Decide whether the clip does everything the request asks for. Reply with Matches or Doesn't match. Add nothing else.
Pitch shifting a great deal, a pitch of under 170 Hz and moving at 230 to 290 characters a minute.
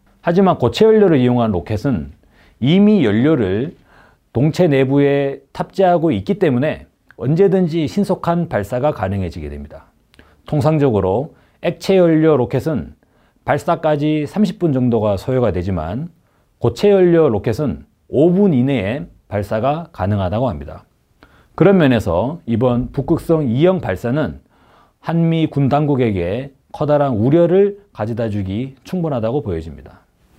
Matches